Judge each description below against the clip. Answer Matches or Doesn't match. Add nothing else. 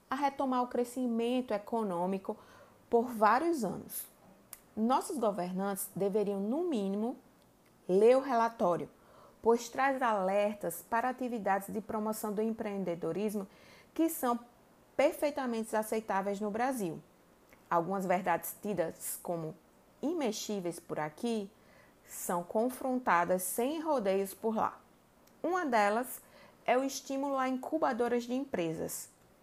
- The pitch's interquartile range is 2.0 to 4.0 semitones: Doesn't match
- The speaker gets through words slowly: Matches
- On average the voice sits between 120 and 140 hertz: Doesn't match